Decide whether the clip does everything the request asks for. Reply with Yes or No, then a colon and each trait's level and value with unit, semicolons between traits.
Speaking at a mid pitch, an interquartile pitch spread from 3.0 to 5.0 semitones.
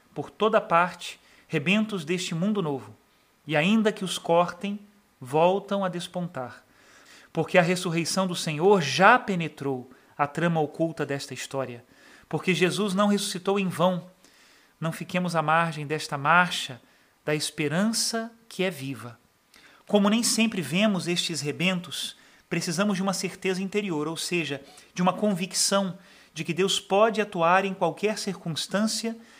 Yes: medium, 180 Hz; average, 4.0 semitones